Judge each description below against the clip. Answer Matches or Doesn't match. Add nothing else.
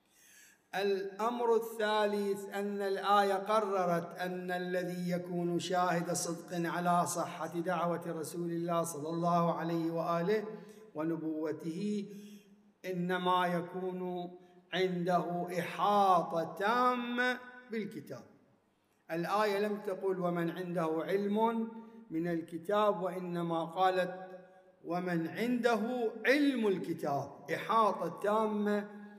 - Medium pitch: Matches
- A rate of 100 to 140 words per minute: Doesn't match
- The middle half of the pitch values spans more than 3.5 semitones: Doesn't match